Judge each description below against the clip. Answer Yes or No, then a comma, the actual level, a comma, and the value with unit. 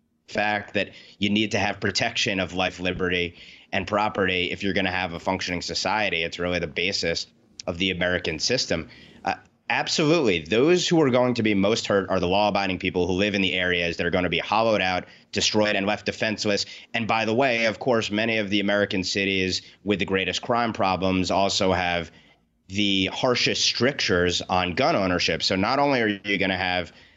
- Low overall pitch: Yes, very low, 95 Hz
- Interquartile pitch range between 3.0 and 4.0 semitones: No, narrow, 2.5 semitones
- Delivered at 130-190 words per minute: No, average, 200 wpm